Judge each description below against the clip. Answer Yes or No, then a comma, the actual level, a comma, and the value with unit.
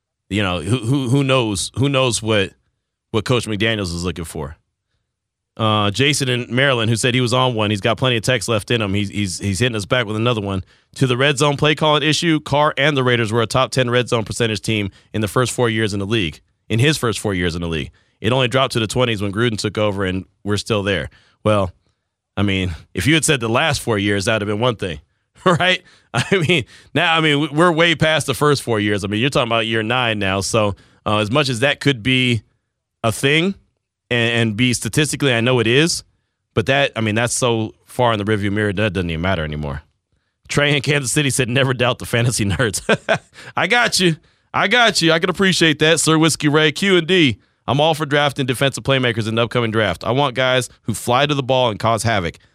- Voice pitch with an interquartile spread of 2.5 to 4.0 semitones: No, average, 4.9 semitones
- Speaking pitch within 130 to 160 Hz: No, low, 120 Hz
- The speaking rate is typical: No, fast, 240 wpm